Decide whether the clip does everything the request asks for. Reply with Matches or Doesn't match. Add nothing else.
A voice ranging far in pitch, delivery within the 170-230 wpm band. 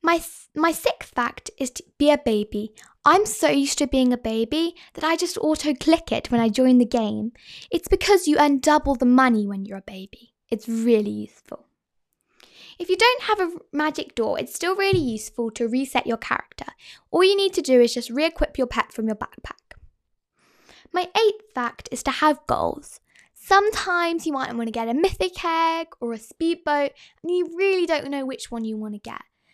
Matches